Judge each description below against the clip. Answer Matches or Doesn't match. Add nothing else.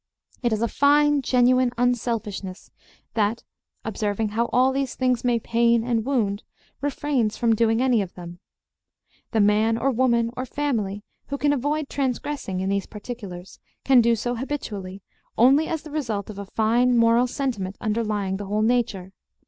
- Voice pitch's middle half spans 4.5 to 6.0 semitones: Doesn't match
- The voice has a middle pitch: Doesn't match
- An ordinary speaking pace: Matches